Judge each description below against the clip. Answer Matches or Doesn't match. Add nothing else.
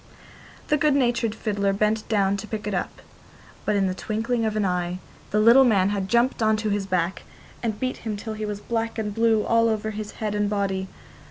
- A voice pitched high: Matches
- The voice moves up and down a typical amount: Doesn't match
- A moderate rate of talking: Doesn't match